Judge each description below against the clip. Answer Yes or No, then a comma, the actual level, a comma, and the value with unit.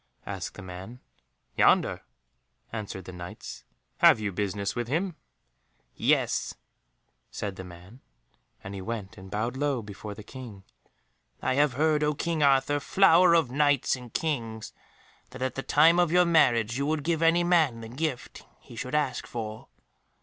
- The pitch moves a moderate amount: No, wide, 6.2 semitones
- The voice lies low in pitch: Yes, low, 125 Hz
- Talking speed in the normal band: Yes, average, 160 wpm